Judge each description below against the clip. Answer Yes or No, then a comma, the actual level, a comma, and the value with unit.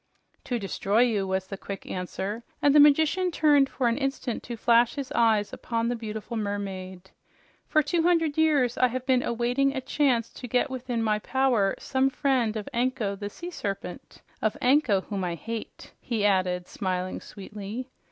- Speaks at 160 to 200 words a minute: Yes, average, 175 wpm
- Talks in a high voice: Yes, high, 235 Hz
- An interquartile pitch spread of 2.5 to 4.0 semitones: No, average, 4.7 semitones